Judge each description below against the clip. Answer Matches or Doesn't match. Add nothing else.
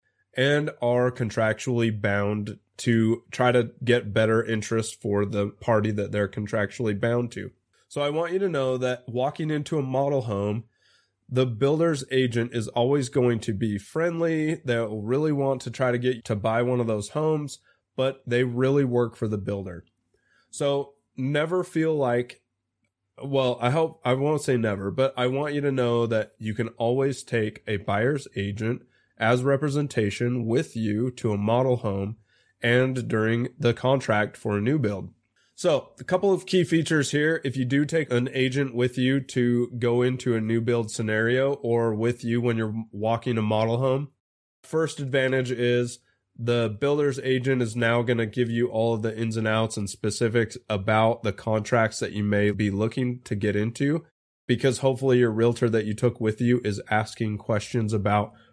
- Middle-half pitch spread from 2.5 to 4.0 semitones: Matches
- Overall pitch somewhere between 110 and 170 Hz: Matches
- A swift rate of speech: Doesn't match